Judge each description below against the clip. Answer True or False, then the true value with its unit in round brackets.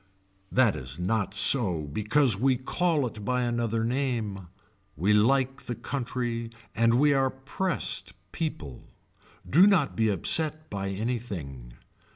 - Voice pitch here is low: True (115 Hz)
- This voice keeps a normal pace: False (130 wpm)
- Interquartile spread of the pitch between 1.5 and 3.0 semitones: False (5.1 semitones)